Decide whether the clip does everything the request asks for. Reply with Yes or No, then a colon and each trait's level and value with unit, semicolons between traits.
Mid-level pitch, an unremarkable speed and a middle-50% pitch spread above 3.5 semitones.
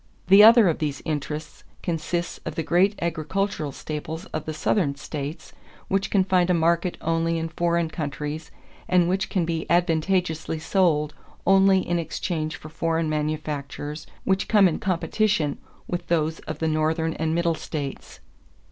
No: medium, 165 Hz; average, 155 wpm; average, 2.7 semitones